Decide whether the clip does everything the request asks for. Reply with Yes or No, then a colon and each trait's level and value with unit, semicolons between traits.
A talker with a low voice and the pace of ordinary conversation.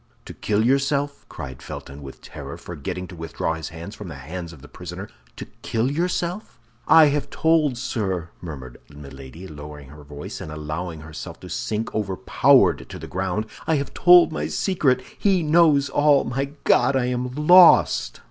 Yes: very low, 95 Hz; average, 170 wpm